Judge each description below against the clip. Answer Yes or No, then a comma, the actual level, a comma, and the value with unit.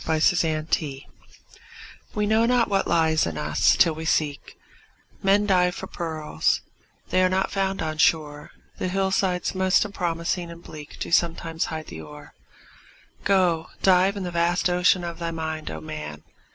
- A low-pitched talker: No, medium, 170 Hz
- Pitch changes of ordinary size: Yes, average, 3.1 semitones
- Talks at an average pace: Yes, average, 155 wpm